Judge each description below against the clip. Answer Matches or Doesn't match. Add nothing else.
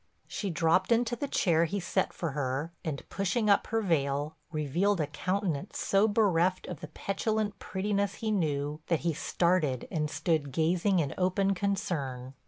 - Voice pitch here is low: Doesn't match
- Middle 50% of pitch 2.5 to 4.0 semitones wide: Doesn't match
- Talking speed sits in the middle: Matches